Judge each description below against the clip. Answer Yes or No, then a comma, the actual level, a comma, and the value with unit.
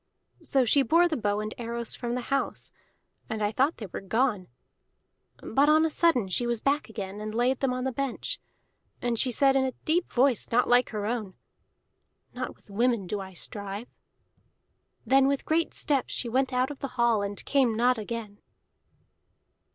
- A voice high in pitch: Yes, high, 245 Hz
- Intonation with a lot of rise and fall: No, average, 4.0 semitones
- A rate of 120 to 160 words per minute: No, average, 185 wpm